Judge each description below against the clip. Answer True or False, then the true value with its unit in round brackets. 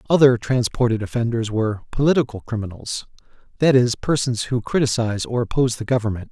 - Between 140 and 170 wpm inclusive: True (145 wpm)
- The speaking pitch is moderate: False (120 Hz)